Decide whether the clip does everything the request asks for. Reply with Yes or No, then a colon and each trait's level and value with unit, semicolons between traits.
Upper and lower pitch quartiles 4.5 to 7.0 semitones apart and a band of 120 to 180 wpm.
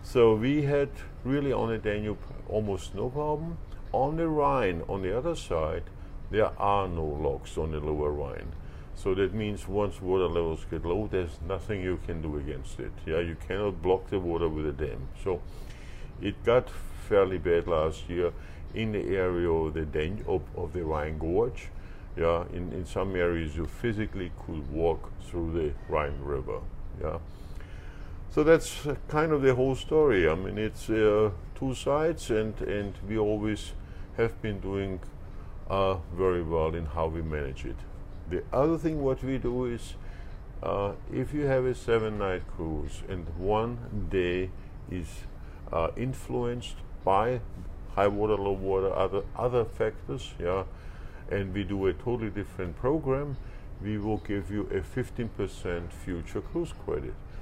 Yes: average, 4.8 semitones; average, 160 wpm